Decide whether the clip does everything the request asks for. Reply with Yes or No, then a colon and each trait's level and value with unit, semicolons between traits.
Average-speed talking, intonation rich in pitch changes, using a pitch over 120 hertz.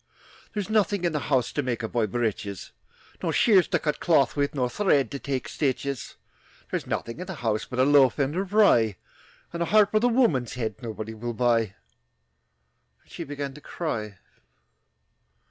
Yes: average, 185 wpm; wide, 6.5 semitones; low, 135 Hz